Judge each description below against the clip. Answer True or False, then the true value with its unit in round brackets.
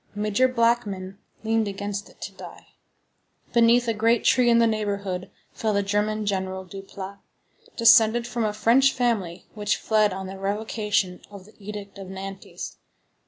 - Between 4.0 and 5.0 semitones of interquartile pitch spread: False (2.7 semitones)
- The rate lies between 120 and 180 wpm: True (155 wpm)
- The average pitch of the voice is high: True (210 Hz)